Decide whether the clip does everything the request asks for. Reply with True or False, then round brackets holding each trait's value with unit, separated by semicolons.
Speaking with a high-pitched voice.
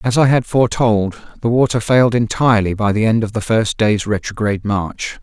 False (110 Hz)